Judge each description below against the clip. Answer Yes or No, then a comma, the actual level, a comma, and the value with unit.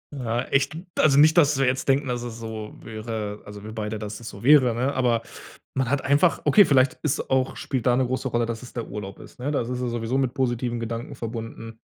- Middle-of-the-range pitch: No, low, 120 Hz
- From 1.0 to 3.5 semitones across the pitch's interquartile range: Yes, average, 2.8 semitones